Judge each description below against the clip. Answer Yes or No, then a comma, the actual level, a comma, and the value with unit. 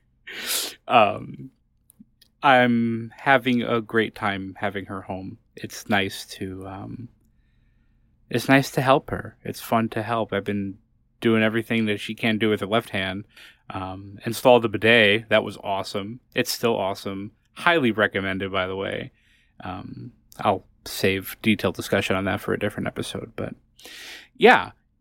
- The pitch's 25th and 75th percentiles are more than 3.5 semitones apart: No, average, 2.9 semitones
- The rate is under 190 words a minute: Yes, average, 150 wpm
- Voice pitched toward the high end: No, low, 110 Hz